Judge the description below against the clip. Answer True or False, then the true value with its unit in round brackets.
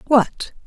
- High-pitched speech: True (235 Hz)